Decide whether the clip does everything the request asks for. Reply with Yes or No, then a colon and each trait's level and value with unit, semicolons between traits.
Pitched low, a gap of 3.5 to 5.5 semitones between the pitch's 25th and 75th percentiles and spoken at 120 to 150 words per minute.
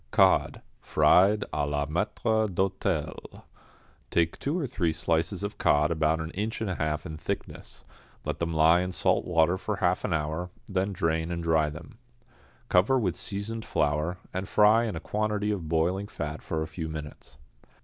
No: very low, 85 Hz; average, 4.4 semitones; average, 175 wpm